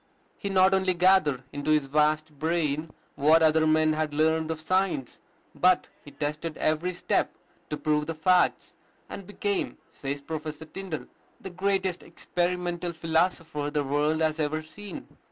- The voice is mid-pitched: Yes, medium, 160 Hz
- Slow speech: No, average, 150 wpm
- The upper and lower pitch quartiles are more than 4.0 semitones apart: No, average, 2.9 semitones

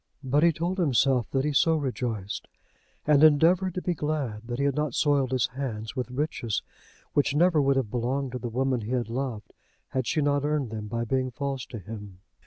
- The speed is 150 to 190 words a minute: No, fast, 205 wpm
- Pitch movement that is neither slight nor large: Yes, average, 3.7 semitones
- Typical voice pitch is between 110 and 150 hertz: Yes, low, 135 Hz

